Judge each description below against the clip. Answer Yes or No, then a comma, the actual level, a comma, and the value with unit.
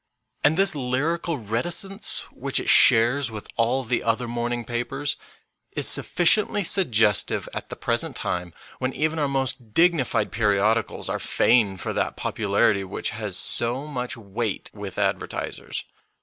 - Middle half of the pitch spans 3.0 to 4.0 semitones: No, average, 5.1 semitones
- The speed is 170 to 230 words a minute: No, average, 145 wpm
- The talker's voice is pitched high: No, low, 120 Hz